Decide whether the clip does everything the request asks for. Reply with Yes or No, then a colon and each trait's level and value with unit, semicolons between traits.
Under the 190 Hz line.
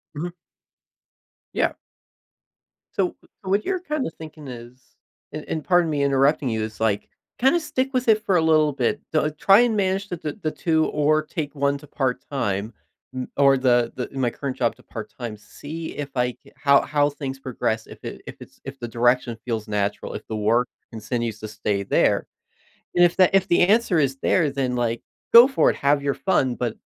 Yes: medium, 140 Hz